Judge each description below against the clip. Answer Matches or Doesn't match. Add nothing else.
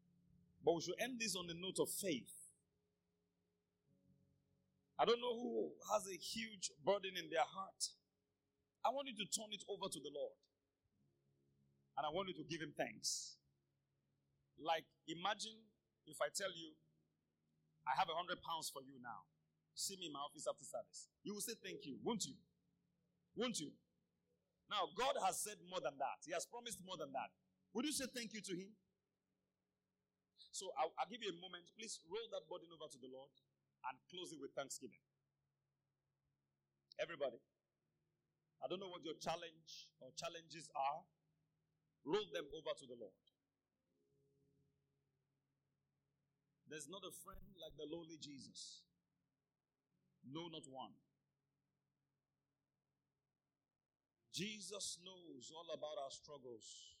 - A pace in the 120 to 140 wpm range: Doesn't match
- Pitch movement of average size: Doesn't match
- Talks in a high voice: Doesn't match